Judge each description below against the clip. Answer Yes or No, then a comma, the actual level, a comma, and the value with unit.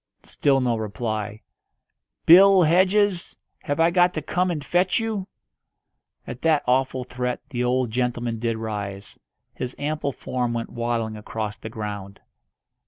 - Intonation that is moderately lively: No, wide, 6.6 semitones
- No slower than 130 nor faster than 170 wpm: Yes, average, 140 wpm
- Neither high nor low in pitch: No, low, 125 Hz